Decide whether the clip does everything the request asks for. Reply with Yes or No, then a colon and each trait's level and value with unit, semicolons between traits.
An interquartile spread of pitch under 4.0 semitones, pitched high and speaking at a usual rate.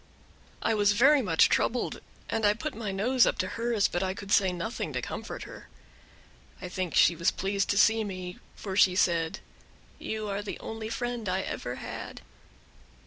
Yes: average, 3.2 semitones; high, 205 Hz; average, 185 wpm